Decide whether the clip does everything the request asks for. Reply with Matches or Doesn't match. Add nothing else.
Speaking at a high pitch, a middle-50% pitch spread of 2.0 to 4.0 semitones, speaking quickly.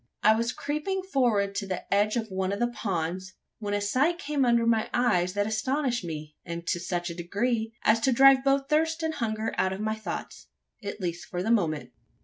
Doesn't match